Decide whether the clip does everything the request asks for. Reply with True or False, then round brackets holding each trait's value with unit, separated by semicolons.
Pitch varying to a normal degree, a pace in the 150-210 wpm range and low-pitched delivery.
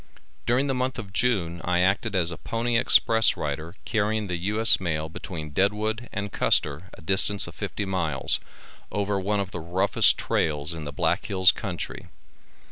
True (4.4 semitones; 170 wpm; 95 Hz)